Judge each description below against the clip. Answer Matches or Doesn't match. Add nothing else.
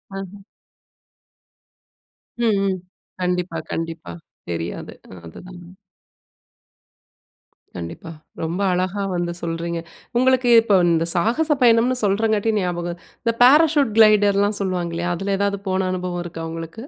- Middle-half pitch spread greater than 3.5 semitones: Matches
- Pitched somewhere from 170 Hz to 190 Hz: Matches